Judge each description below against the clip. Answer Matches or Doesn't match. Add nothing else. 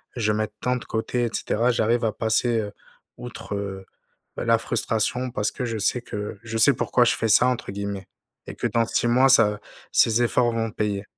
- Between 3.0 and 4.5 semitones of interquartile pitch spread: Doesn't match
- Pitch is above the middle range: Doesn't match